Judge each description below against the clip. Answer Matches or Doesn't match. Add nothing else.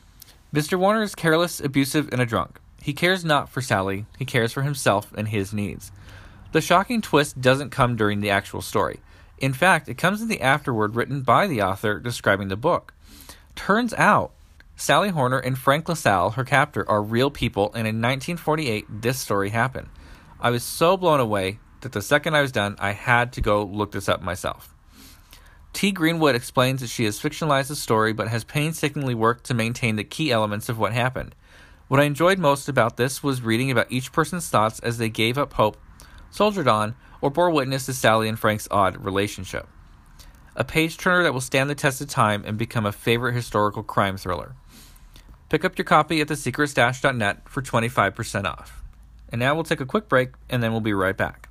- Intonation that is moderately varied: Doesn't match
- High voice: Doesn't match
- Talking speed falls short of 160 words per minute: Doesn't match